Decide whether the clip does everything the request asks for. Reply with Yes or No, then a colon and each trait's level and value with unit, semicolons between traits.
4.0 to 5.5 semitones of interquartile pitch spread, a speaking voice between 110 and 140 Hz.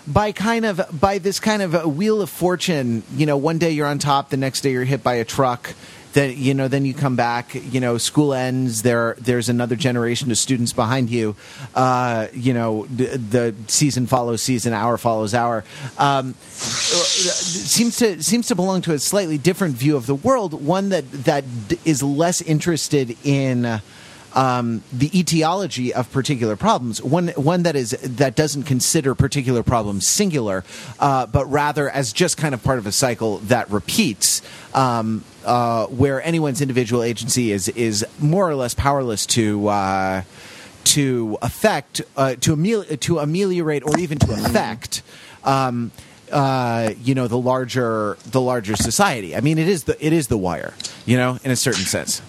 Yes: average, 4.5 semitones; low, 135 Hz